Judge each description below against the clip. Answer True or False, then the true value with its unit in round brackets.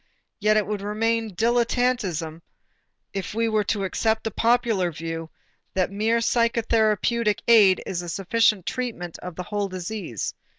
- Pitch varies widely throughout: False (3.7 semitones)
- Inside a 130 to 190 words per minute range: True (145 wpm)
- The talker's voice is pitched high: True (210 Hz)